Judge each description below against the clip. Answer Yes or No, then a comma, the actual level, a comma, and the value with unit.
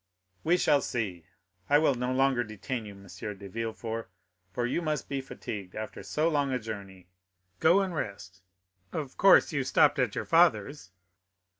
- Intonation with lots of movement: Yes, wide, 5.9 semitones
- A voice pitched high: No, low, 120 Hz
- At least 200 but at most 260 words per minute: No, average, 165 wpm